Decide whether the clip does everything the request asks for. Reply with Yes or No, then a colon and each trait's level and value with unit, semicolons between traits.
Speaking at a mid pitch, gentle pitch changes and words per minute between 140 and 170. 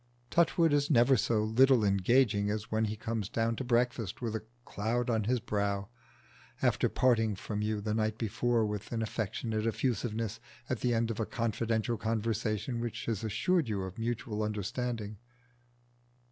No: low, 115 Hz; narrow, 2.0 semitones; average, 160 wpm